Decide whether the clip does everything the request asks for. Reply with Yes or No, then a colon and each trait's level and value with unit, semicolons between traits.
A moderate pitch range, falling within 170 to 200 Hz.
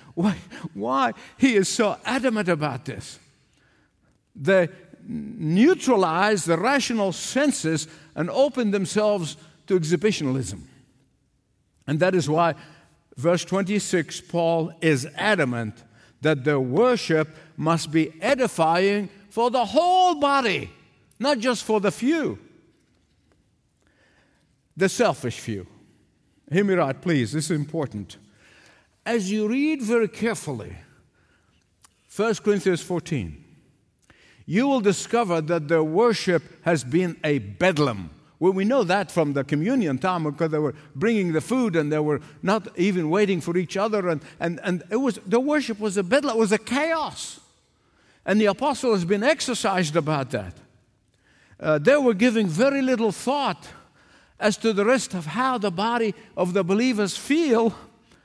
No: wide, 6.4 semitones; medium, 185 Hz